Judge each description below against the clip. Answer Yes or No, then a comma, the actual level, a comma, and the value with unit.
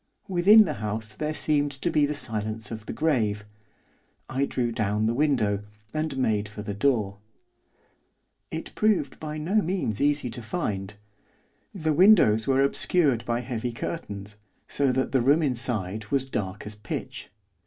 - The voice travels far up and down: Yes, wide, 6.0 semitones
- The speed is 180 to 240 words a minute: No, average, 155 wpm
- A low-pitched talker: Yes, low, 125 Hz